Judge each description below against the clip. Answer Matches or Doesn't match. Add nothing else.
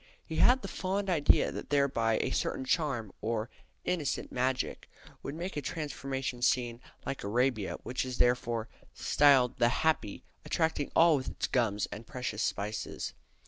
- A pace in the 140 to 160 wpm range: Matches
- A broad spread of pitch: Doesn't match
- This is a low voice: Matches